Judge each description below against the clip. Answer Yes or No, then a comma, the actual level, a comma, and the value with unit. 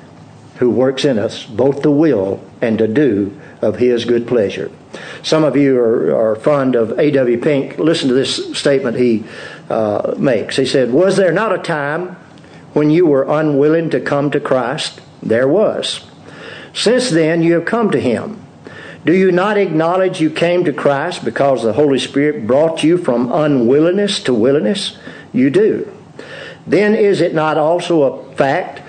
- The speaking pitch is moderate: Yes, medium, 150 Hz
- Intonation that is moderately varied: Yes, average, 4.8 semitones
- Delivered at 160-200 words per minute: Yes, average, 170 wpm